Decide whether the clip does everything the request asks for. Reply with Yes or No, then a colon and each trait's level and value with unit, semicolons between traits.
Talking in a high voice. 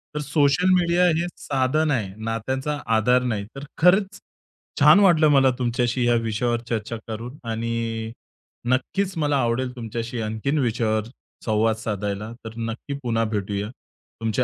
No: low, 120 Hz